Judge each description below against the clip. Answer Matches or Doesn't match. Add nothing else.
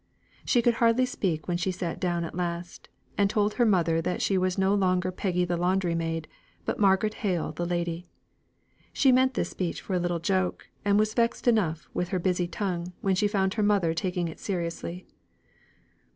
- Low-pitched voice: Doesn't match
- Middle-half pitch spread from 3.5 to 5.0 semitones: Doesn't match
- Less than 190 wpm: Doesn't match